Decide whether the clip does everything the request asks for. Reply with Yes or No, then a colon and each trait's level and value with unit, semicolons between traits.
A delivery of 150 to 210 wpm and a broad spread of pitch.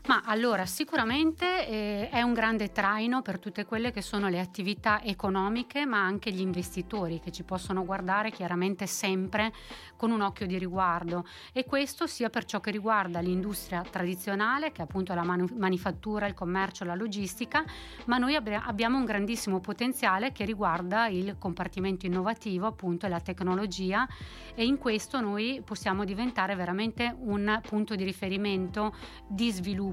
No: average, 160 wpm; average, 3.2 semitones